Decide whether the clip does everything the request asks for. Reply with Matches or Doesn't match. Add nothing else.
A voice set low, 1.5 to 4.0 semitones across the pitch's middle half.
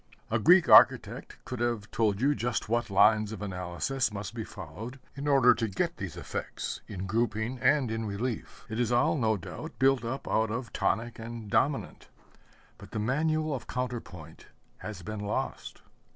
Matches